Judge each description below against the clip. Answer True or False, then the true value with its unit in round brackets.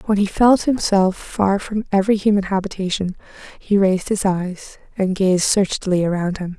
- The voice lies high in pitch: True (195 Hz)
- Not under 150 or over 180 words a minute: True (165 wpm)